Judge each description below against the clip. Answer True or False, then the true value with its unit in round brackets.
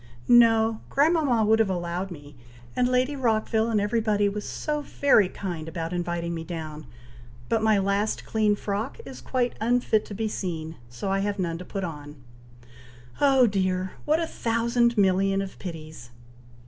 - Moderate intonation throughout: True (4.6 semitones)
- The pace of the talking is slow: False (165 wpm)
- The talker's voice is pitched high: True (205 Hz)